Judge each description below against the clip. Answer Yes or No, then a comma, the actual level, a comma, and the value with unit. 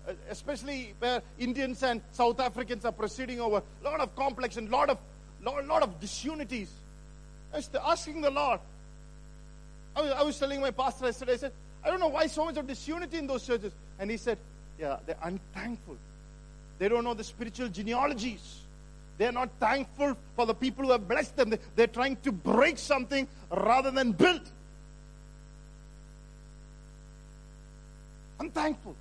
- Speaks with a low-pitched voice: No, very high, 255 Hz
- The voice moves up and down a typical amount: Yes, average, 3.8 semitones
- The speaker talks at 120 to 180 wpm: Yes, average, 155 wpm